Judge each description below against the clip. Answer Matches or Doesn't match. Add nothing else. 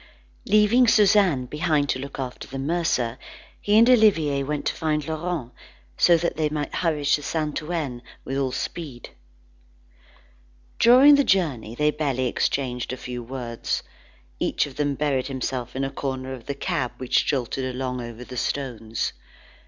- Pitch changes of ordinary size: Matches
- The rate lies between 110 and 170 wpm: Matches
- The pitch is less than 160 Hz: Matches